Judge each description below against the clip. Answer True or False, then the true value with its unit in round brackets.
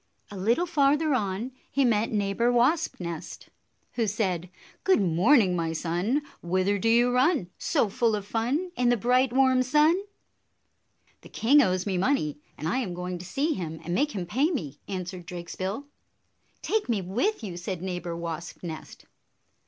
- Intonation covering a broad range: True (6.4 semitones)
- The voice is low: False (210 Hz)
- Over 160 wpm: True (170 wpm)